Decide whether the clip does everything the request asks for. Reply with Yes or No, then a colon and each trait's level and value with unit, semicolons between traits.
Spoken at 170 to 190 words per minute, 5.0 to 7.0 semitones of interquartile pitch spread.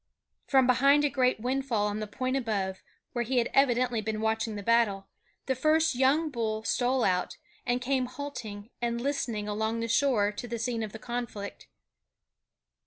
No: average, 175 wpm; average, 3.3 semitones